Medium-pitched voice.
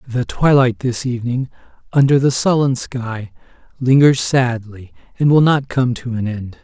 No: low, 125 Hz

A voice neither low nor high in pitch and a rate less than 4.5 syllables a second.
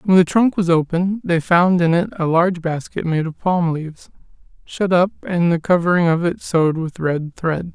No: medium, 170 Hz; 5.1 syllables/s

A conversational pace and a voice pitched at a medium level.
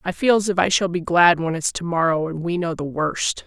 No: fast, 295 wpm; medium, 170 Hz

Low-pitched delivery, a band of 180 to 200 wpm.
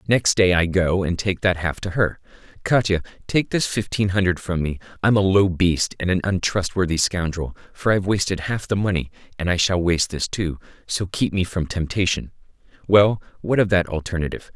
Yes: very low, 90 Hz; average, 195 wpm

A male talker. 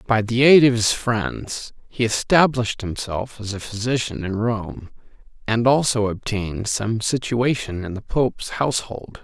Yes: male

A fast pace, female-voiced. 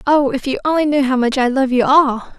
Yes: fast, 275 wpm; female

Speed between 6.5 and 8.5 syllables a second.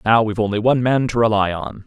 No: 6.3 syllables/s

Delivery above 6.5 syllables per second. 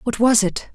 No: 4.8 syllables/s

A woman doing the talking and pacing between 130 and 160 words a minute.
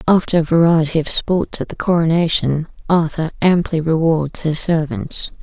Yes: female; average, 145 wpm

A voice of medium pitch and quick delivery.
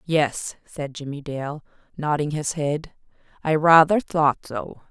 No: medium, 150 Hz; slow, 135 wpm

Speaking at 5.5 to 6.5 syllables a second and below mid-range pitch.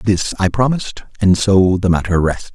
No: 5.0 syllables/s; low, 100 Hz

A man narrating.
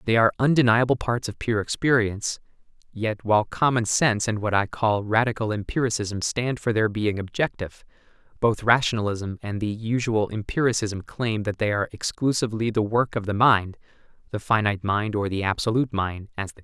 Yes: male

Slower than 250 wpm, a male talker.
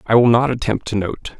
No: fast, 260 wpm; male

